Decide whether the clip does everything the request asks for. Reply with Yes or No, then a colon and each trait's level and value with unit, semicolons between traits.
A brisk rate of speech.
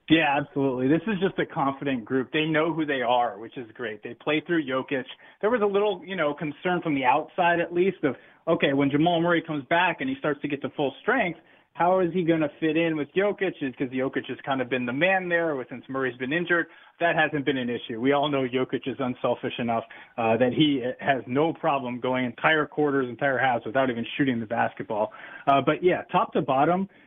Yes: fast, 230 wpm